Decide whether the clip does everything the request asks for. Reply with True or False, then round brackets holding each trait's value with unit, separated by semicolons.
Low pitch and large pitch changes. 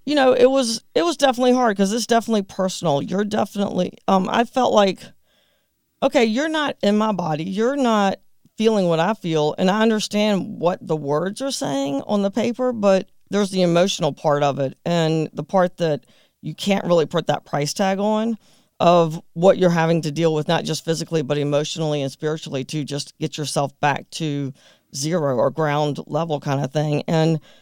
False (175 Hz; 5.8 semitones)